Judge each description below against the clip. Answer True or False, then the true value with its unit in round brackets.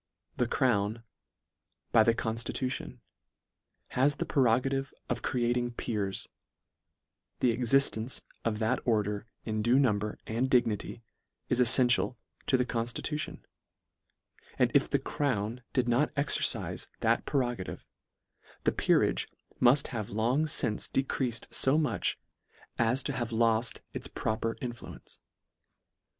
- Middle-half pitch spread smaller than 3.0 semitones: True (2.5 semitones)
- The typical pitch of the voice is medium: False (120 Hz)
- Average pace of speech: False (120 wpm)